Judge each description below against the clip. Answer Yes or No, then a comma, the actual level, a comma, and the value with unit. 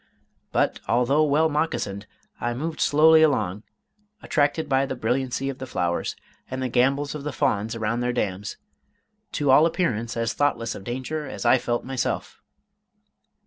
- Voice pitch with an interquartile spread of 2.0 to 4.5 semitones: Yes, average, 3.9 semitones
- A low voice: Yes, low, 130 Hz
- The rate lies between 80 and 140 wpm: No, average, 155 wpm